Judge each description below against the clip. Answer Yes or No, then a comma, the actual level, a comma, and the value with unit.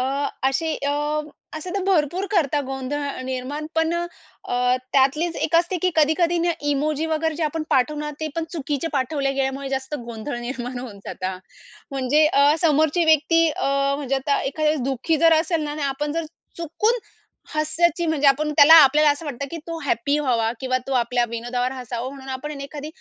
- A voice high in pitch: Yes, very high, 290 Hz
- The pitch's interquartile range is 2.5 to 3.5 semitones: Yes, average, 3.1 semitones